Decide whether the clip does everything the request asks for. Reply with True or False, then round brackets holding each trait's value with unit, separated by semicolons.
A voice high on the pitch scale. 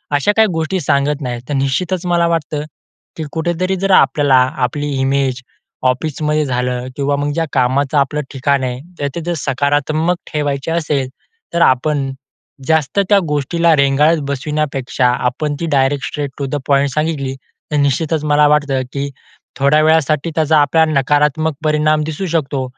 False (145 Hz)